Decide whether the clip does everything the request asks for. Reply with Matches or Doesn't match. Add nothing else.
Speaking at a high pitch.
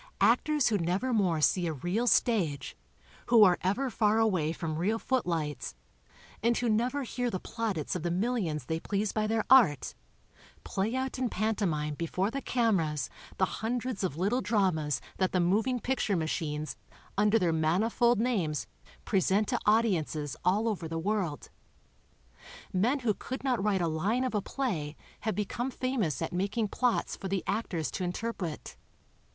Matches